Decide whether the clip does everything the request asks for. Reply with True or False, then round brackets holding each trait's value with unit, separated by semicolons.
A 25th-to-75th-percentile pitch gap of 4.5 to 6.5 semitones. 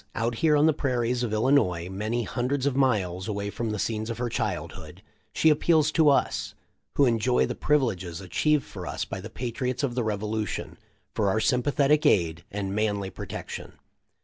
True (5.1 semitones)